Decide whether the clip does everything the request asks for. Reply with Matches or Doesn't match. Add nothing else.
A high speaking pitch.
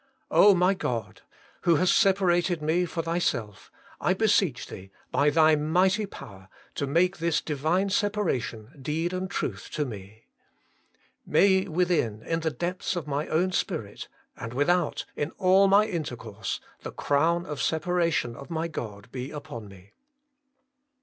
Doesn't match